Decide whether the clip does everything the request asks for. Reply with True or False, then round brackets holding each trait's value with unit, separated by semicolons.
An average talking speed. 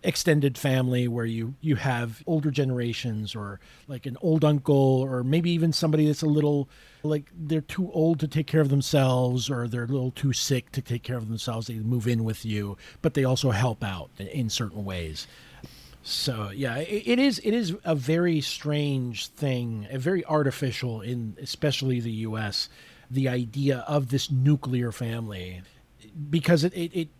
True (180 wpm)